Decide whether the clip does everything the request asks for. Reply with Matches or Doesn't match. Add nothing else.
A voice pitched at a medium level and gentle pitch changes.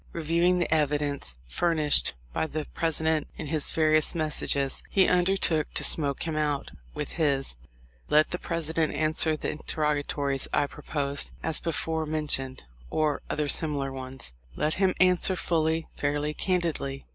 Matches